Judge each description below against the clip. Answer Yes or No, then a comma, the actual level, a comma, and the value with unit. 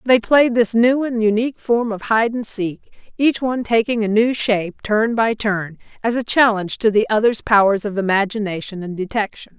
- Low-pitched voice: No, high, 220 Hz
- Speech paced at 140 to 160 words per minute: No, average, 195 wpm